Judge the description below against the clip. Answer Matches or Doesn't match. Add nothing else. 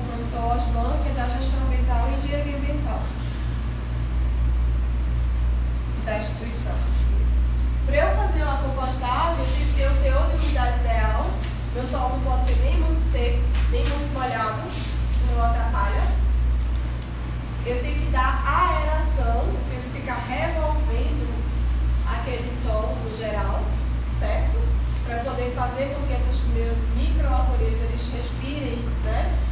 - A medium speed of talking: Doesn't match